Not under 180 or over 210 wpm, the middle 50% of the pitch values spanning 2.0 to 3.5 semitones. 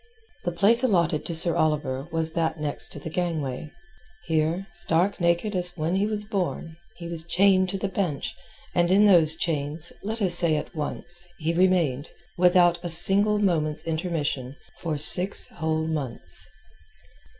No: average, 155 wpm; average, 2.8 semitones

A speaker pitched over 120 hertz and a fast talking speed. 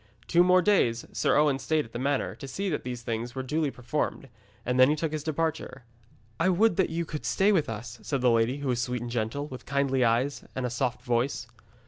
Yes: low, 135 Hz; fast, 230 wpm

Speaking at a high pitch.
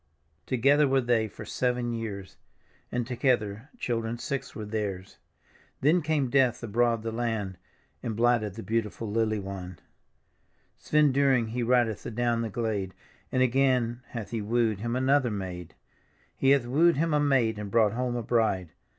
No: low, 115 Hz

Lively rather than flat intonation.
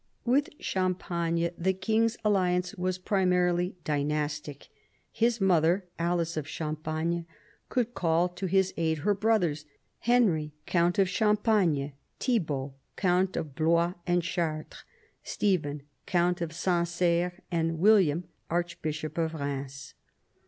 No: average, 3.1 semitones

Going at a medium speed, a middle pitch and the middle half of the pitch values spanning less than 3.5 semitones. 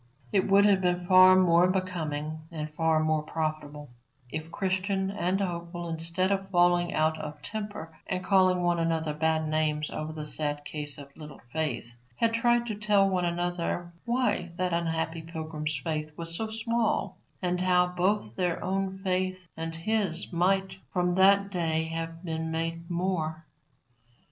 Yes: average, 160 wpm; medium, 175 Hz; average, 2.8 semitones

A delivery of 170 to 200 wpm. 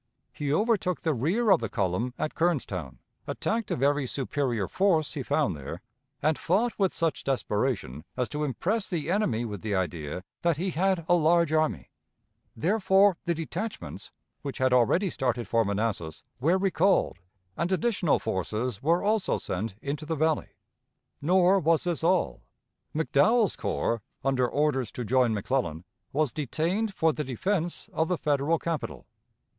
No: average, 155 wpm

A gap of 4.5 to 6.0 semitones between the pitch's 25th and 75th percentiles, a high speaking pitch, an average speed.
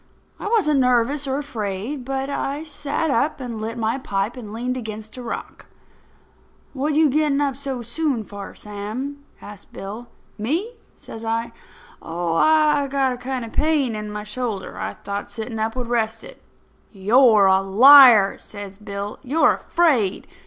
Yes: average, 4.9 semitones; high, 240 Hz; average, 165 wpm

